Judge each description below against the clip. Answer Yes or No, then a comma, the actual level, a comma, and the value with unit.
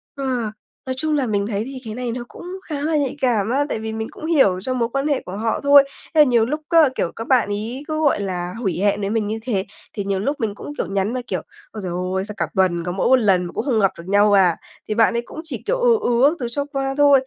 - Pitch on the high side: Yes, high, 230 Hz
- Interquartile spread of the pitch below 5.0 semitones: No, wide, 5.6 semitones